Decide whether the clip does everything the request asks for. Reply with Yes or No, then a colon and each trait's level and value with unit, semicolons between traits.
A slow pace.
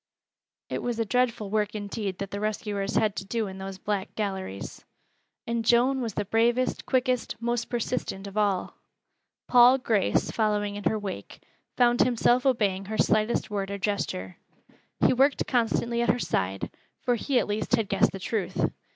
No: average, 170 wpm